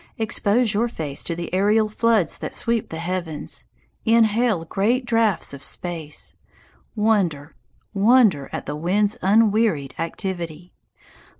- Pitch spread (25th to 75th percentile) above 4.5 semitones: Yes, average, 5.1 semitones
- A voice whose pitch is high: Yes, high, 200 Hz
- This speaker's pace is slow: Yes, slow, 120 wpm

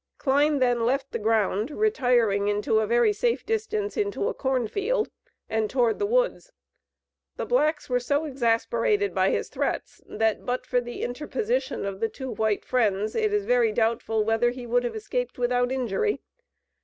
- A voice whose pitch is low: No, very high, 250 Hz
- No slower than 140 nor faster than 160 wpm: No, average, 170 wpm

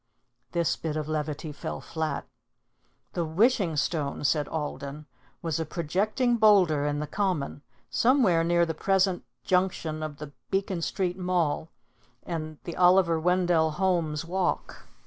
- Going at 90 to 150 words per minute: Yes, slow, 135 wpm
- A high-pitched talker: No, medium, 165 Hz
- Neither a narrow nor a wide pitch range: Yes, average, 3.2 semitones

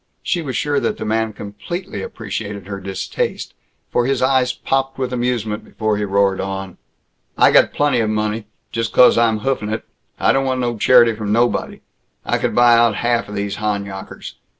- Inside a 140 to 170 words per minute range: No, average, 180 wpm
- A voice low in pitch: Yes, low, 110 Hz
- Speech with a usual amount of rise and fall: Yes, average, 3.3 semitones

